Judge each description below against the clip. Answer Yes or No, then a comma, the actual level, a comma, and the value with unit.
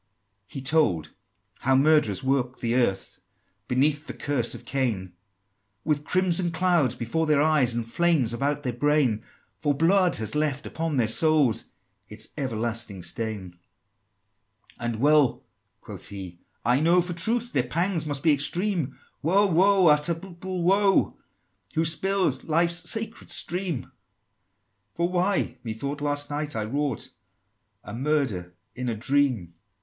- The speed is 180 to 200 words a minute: No, average, 140 wpm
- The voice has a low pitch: No, medium, 145 Hz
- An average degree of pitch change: No, wide, 5.9 semitones